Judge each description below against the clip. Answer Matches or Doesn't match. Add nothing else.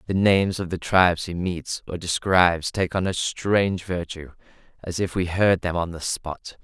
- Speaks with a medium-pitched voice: Doesn't match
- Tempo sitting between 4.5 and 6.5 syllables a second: Matches